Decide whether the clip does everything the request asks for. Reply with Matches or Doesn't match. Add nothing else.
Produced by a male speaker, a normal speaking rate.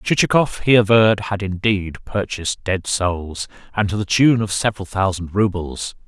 Matches